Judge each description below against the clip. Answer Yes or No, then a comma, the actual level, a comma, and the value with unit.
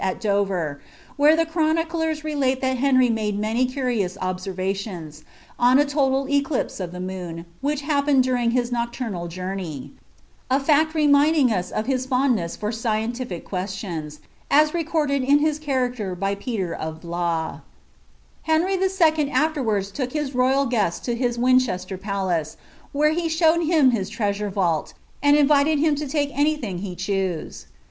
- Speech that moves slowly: No, average, 155 wpm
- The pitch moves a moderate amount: No, wide, 7.1 semitones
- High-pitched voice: Yes, very high, 250 Hz